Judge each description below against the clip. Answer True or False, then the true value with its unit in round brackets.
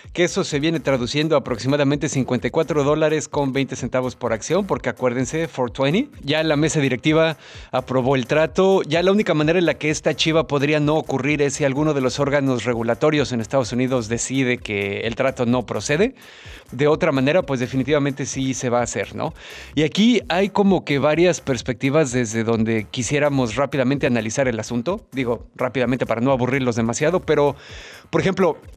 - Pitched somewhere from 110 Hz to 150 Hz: True (140 Hz)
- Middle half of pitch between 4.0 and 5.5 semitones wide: False (3.6 semitones)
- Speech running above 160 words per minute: True (180 wpm)